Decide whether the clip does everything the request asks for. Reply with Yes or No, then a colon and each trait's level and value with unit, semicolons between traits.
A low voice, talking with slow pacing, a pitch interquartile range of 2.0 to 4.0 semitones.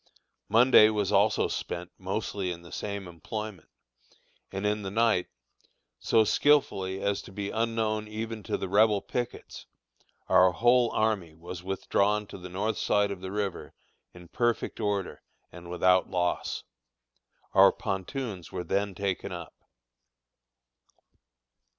Yes: low, 100 Hz; slow, 130 wpm; average, 2.8 semitones